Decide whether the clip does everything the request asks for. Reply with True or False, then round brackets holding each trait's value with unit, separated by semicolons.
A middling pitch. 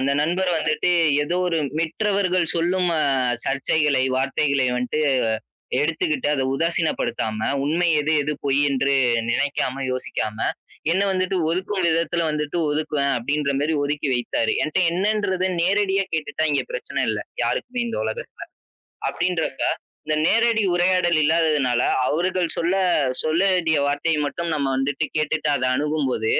True (155 Hz)